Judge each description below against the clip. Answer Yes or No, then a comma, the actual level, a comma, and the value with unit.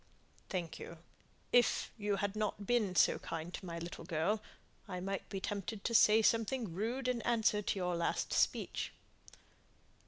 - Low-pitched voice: No, high, 200 Hz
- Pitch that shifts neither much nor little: Yes, average, 3.7 semitones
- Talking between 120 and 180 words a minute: Yes, average, 155 wpm